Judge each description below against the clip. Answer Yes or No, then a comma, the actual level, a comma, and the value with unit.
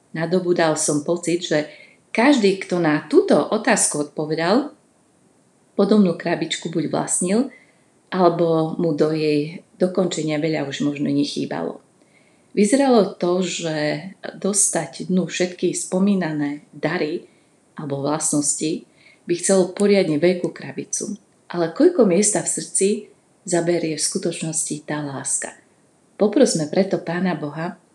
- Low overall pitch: No, medium, 175 Hz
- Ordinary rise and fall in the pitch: Yes, average, 3.8 semitones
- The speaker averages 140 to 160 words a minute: No, average, 115 wpm